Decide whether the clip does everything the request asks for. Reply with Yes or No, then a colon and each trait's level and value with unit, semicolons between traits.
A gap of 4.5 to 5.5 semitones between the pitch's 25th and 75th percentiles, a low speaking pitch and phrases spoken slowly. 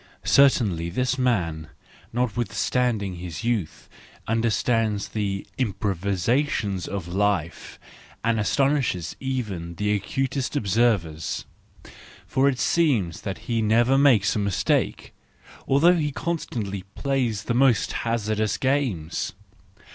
Yes: average, 4.8 semitones; low, 110 Hz; slow, 105 wpm